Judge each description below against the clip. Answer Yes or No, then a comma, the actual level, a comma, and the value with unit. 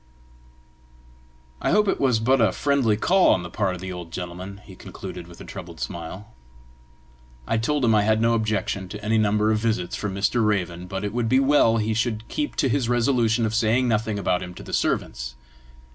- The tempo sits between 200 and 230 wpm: Yes, fast, 205 wpm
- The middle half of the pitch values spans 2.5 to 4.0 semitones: Yes, average, 3.7 semitones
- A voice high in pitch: No, low, 110 Hz